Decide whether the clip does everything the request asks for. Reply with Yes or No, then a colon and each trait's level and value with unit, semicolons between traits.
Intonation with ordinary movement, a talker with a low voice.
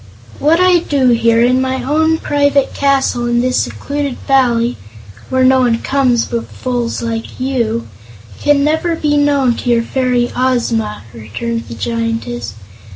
No: average, 3.3 semitones; very high, 255 Hz